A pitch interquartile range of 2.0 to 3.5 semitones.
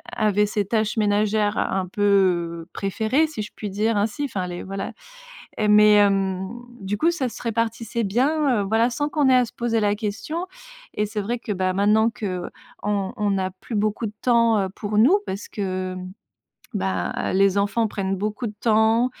Yes: average, 2.7 semitones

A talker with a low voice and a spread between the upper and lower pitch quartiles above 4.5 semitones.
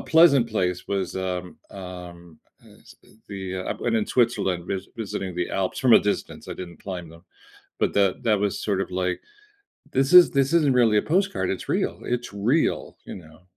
Yes: low, 100 Hz; average, 4.9 semitones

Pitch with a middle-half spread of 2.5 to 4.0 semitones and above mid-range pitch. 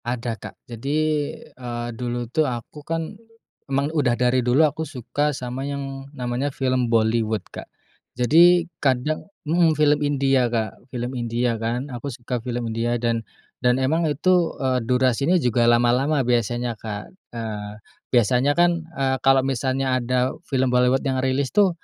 No: average, 2.9 semitones; low, 130 Hz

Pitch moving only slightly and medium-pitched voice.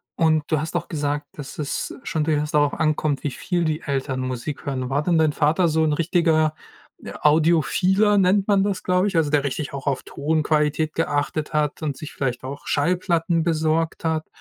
Yes: narrow, 2.3 semitones; medium, 155 Hz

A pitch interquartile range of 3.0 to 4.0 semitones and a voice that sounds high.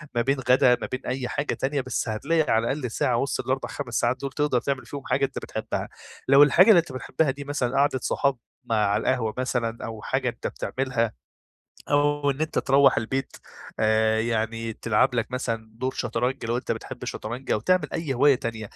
No: average, 3.3 semitones; low, 130 Hz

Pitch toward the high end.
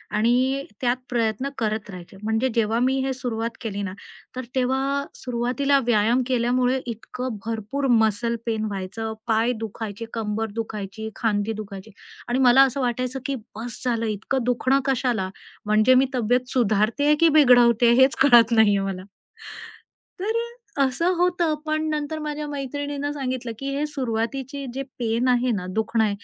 Yes: high, 245 Hz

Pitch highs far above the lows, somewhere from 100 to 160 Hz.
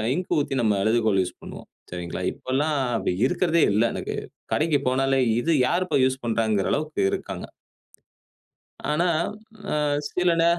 Yes: wide, 6.4 semitones; low, 135 Hz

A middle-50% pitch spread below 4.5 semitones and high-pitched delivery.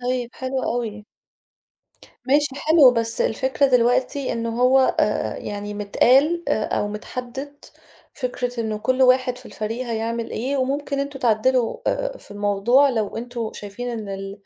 Yes: average, 3.2 semitones; high, 245 Hz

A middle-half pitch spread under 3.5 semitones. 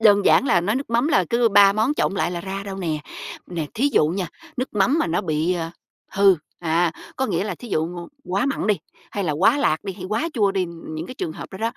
No: average, 4.4 semitones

